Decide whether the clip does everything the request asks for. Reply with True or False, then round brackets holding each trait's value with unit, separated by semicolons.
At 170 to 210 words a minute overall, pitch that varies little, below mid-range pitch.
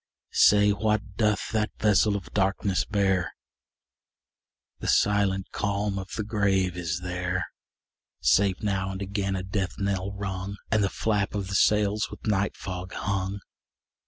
False (145 wpm; 1.5 semitones; 100 Hz)